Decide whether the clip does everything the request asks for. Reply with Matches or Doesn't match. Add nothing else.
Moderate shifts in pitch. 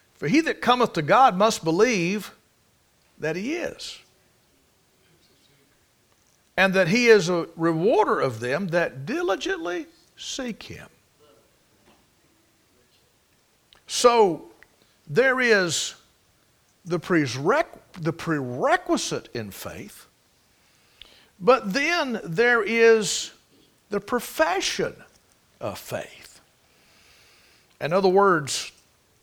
Doesn't match